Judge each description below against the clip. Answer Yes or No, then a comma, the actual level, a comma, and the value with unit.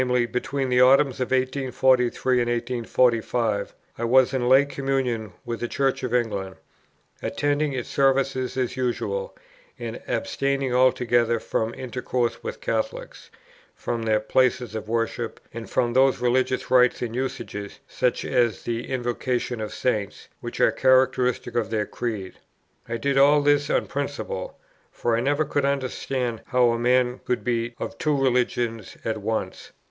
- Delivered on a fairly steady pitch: Yes, narrow, 2.3 semitones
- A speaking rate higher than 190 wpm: No, average, 150 wpm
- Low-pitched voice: Yes, low, 125 Hz